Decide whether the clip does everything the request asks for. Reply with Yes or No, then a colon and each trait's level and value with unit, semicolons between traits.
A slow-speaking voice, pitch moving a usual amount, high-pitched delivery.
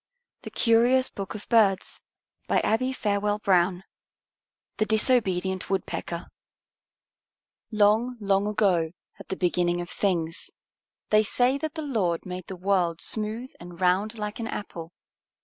Yes: slow, 120 wpm; average, 3.6 semitones; high, 200 Hz